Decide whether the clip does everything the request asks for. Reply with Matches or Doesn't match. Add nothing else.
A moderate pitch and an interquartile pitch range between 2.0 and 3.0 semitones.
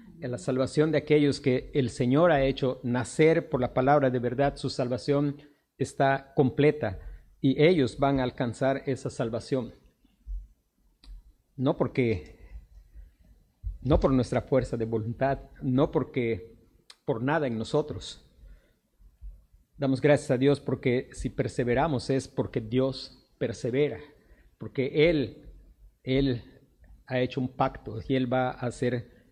Doesn't match